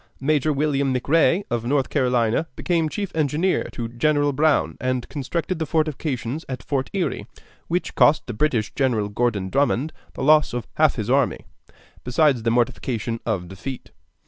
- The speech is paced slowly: No, average, 155 wpm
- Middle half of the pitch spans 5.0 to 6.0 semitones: No, average, 4.4 semitones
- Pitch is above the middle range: No, low, 135 Hz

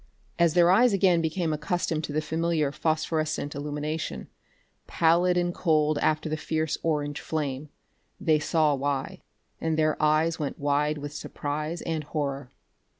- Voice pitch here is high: No, medium, 155 Hz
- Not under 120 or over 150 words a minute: Yes, average, 145 wpm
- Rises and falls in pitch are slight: Yes, narrow, 1.9 semitones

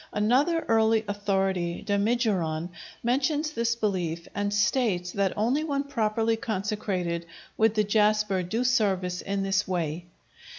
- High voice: Yes, high, 210 Hz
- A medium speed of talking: No, slow, 125 wpm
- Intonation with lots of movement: No, average, 3.5 semitones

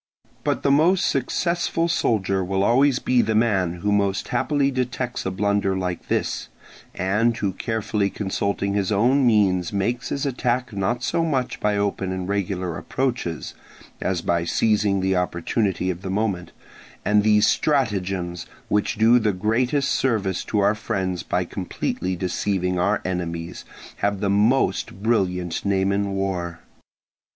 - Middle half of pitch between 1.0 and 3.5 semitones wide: No, average, 4.1 semitones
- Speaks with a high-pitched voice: No, low, 100 Hz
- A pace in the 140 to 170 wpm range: Yes, average, 150 wpm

